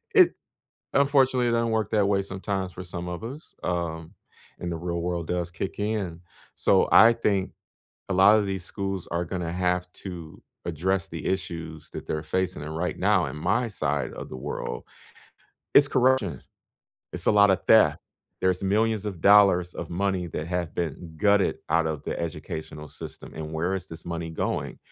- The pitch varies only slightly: No, average, 3.3 semitones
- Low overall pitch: Yes, very low, 90 Hz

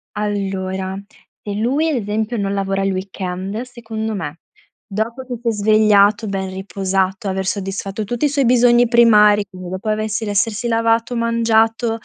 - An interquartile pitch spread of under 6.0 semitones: Yes, average, 2.9 semitones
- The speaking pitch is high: Yes, high, 210 Hz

